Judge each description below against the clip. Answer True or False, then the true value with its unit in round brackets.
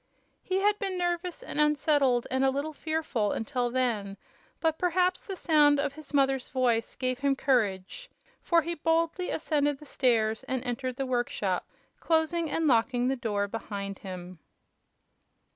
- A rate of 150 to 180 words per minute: True (155 wpm)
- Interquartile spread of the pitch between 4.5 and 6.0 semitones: True (5.0 semitones)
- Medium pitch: False (270 Hz)